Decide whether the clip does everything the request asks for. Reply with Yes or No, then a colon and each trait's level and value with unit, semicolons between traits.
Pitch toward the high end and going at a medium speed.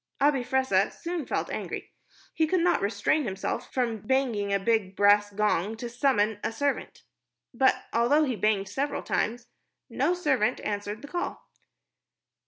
Yes: high, 230 Hz; average, 150 wpm